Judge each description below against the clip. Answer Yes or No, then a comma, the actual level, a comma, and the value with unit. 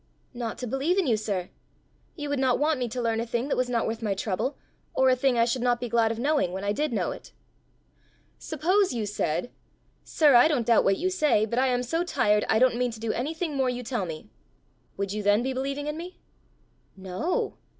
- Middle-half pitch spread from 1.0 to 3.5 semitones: No, average, 4.4 semitones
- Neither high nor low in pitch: No, high, 245 Hz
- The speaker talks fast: Yes, fast, 235 wpm